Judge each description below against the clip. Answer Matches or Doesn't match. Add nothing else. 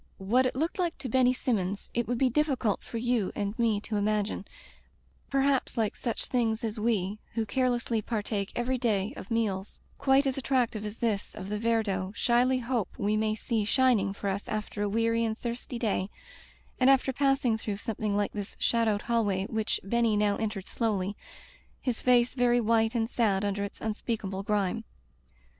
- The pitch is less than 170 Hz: Doesn't match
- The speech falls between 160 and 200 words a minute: Matches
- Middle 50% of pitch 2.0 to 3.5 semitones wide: Matches